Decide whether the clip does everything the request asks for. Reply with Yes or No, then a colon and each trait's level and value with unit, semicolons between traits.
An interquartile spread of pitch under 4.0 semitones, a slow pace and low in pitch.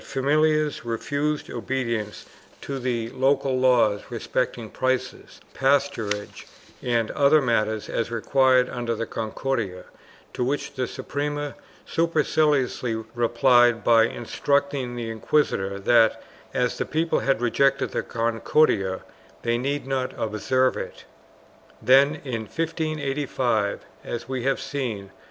Yes: average, 3.5 semitones; slow, 120 wpm; low, 125 Hz